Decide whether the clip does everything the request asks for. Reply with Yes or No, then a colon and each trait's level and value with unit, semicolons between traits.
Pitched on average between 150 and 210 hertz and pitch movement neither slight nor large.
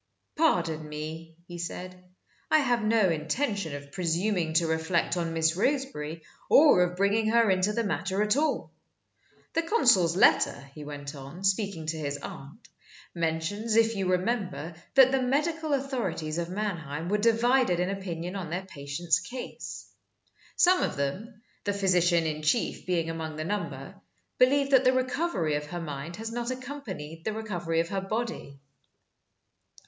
No: medium, 185 Hz; wide, 6.0 semitones